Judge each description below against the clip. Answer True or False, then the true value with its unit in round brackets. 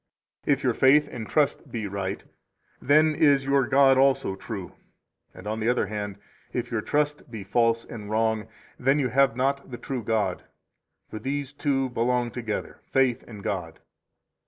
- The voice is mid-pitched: False (125 Hz)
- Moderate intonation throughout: True (4.0 semitones)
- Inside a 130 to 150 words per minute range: False (170 wpm)